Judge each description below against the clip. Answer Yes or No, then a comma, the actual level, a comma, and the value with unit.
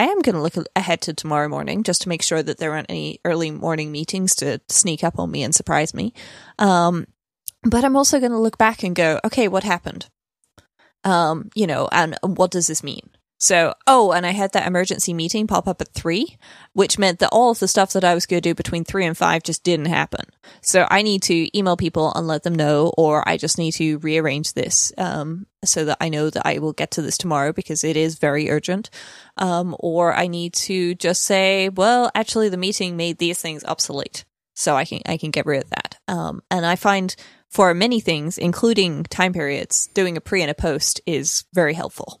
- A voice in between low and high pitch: Yes, medium, 175 Hz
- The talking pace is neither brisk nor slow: No, fast, 225 wpm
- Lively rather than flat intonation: No, average, 3.4 semitones